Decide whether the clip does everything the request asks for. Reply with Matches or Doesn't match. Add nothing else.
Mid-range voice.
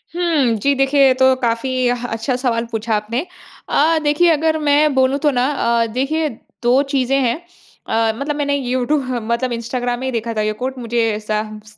Doesn't match